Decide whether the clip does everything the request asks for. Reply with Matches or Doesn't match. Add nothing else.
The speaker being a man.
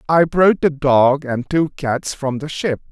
Matches